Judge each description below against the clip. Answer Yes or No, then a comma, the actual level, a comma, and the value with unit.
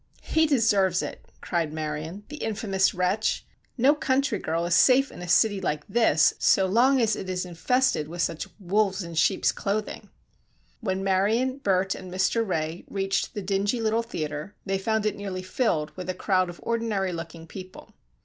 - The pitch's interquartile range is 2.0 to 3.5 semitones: No, average, 4.0 semitones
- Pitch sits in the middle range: No, high, 195 Hz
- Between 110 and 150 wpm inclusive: No, average, 175 wpm